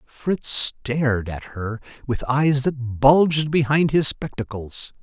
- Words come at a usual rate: No, slow, 130 wpm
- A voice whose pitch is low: Yes, low, 130 Hz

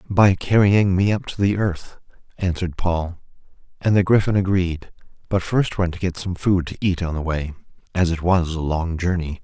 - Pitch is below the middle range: Yes, very low, 90 Hz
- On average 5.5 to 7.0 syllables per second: No, 5.0 syllables/s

